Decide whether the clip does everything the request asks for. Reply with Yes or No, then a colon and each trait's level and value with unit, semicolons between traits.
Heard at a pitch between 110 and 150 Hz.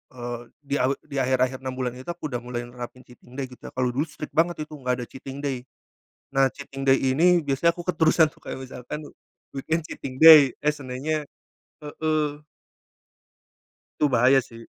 Yes: low, 135 Hz